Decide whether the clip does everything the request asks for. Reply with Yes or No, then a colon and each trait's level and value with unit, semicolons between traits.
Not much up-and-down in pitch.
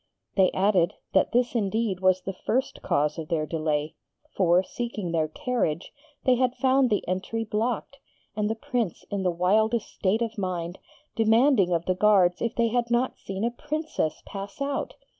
No: average, 4.8 semitones